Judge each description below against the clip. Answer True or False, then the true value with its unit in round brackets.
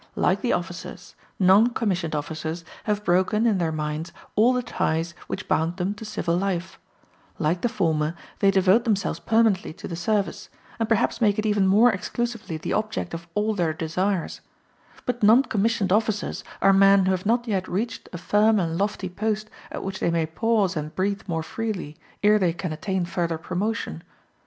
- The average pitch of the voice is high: True (195 Hz)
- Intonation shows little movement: False (4.0 semitones)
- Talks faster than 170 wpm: True (180 wpm)